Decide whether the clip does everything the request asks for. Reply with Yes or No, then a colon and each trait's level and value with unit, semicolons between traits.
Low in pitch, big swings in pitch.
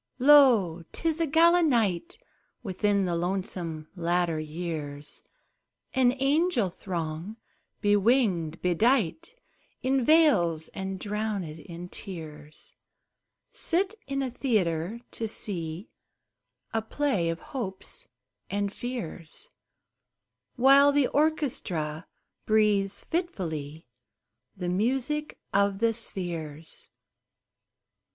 No: high, 200 Hz; wide, 7.7 semitones